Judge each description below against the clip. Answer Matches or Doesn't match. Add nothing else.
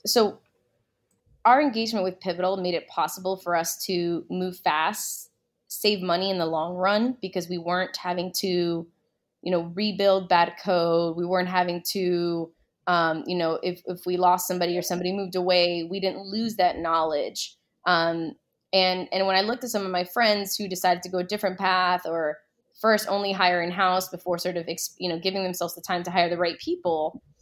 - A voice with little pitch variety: Matches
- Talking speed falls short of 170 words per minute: Doesn't match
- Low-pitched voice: Doesn't match